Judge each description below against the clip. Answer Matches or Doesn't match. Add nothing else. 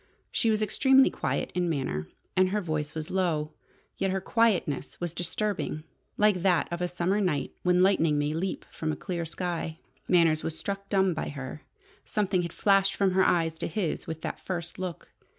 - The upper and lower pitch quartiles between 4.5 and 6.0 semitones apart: Doesn't match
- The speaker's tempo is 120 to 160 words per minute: Doesn't match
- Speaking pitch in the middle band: Matches